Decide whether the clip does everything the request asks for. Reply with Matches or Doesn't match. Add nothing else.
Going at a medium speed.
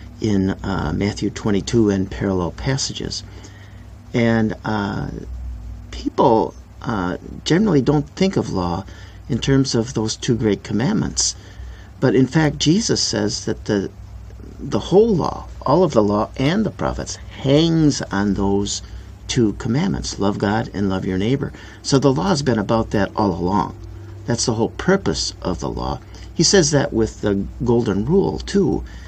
Matches